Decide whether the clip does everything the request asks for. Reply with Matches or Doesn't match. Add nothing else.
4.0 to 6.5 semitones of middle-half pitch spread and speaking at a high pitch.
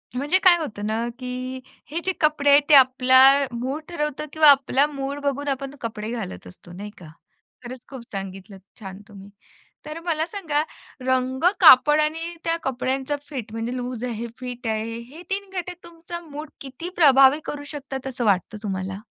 Matches